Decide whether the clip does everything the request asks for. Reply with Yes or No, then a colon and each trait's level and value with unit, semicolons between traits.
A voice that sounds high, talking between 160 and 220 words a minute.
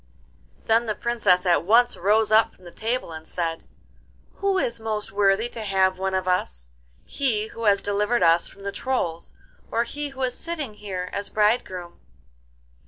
Yes: high, 205 Hz; average, 170 wpm